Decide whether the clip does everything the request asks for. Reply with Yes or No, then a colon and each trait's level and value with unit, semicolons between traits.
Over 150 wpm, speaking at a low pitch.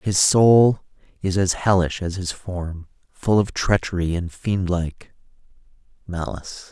No: slow, 135 wpm; very low, 90 Hz